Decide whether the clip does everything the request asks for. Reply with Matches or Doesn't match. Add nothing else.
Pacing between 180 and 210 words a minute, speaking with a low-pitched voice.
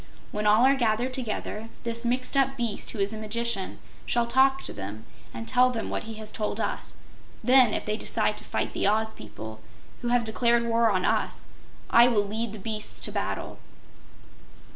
Doesn't match